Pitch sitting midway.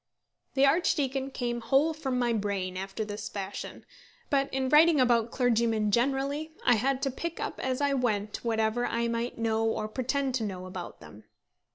No: high, 240 Hz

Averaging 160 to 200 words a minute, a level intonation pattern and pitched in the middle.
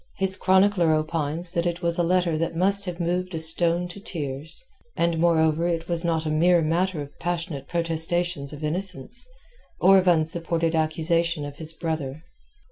Yes: average, 170 wpm; narrow, 1.9 semitones; medium, 170 Hz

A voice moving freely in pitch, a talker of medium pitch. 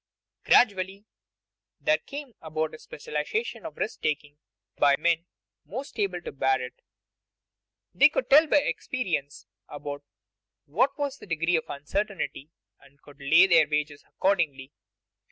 Yes: wide, 6.3 semitones; medium, 165 Hz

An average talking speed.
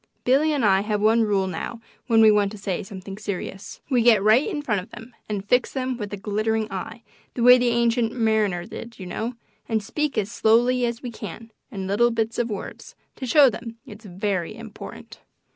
No: fast, 210 wpm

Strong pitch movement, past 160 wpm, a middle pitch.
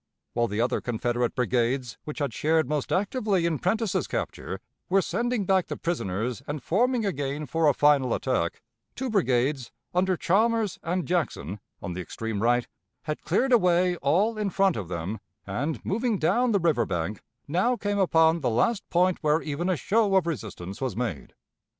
Yes: wide, 7.9 semitones; average, 175 wpm; medium, 160 Hz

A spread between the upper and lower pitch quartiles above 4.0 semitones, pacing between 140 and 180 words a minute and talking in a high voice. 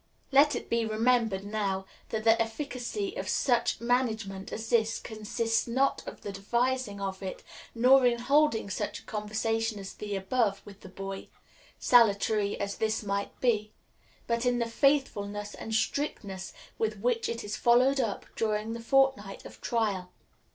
No: average, 3.1 semitones; average, 160 wpm; high, 225 Hz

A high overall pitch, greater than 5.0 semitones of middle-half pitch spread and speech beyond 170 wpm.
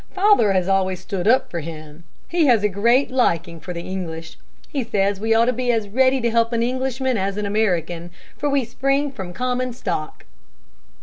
Yes: high, 220 Hz; wide, 5.6 semitones; average, 195 wpm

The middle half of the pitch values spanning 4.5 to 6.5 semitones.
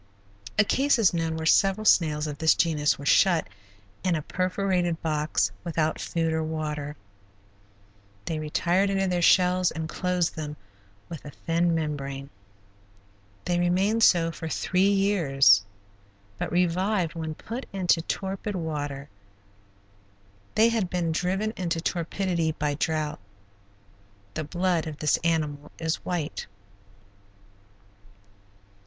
No: average, 3.0 semitones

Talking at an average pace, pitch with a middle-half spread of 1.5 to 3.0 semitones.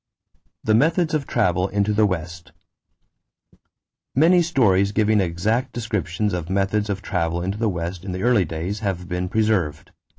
No: average, 155 wpm; average, 3.6 semitones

